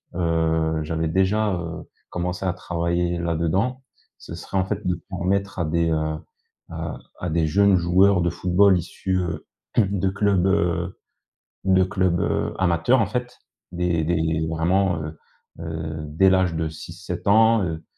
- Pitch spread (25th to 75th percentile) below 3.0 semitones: Yes, narrow, 2.6 semitones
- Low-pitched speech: Yes, very low, 90 Hz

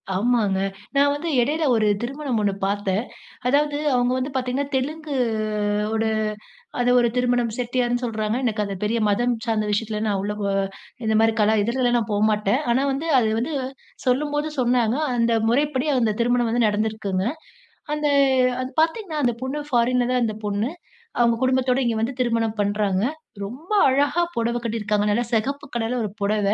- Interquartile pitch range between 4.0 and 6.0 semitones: No, average, 3.3 semitones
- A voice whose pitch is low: No, high, 240 Hz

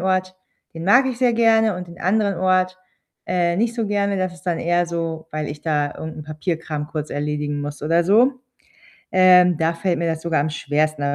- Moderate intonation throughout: Yes, average, 3.4 semitones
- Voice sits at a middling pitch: Yes, medium, 175 Hz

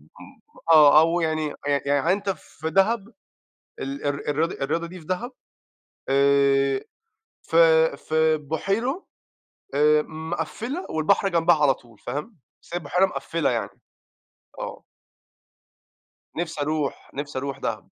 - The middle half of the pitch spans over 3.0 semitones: Yes, average, 3.5 semitones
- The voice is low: No, medium, 160 Hz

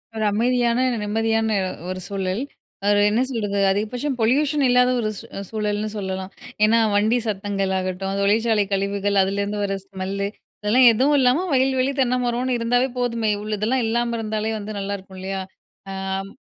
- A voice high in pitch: Yes, high, 215 Hz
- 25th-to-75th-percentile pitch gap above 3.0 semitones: Yes, average, 3.4 semitones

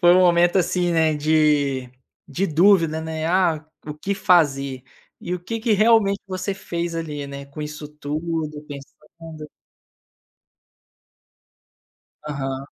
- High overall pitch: No, medium, 160 Hz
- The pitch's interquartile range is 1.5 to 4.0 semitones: Yes, average, 3.1 semitones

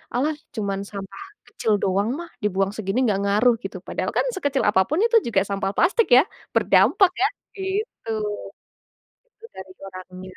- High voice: Yes, high, 210 Hz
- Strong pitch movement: Yes, wide, 8.3 semitones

